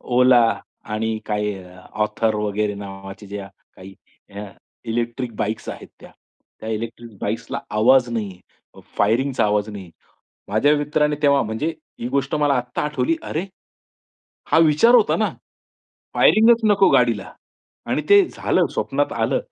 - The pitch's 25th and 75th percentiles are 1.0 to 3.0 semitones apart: No, wide, 5.5 semitones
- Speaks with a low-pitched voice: Yes, low, 115 Hz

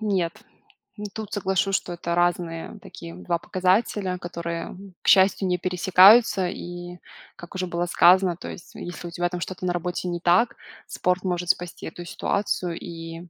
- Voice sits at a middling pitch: Yes, medium, 175 Hz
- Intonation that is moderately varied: No, narrow, 1.5 semitones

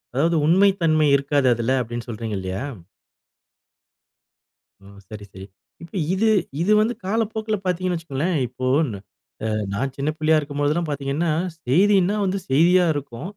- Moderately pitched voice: Yes, medium, 155 Hz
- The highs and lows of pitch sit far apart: Yes, wide, 5.7 semitones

